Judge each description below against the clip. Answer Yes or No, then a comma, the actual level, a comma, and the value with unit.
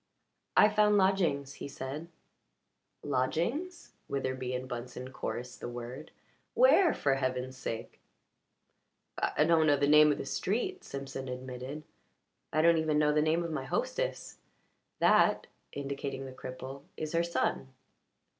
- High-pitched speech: No, medium, 140 Hz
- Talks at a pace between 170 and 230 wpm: No, slow, 135 wpm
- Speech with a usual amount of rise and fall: Yes, average, 4.4 semitones